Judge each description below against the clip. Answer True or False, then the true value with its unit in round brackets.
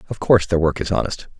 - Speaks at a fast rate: True (260 wpm)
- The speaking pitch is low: True (90 Hz)